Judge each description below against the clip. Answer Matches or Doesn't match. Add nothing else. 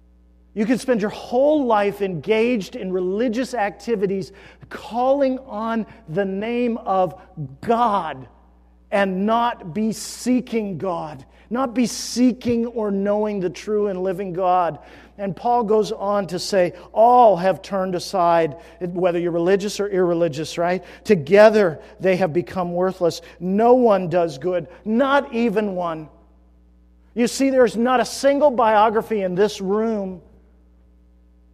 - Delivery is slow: Matches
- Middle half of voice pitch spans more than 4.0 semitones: Matches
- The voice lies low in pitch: Doesn't match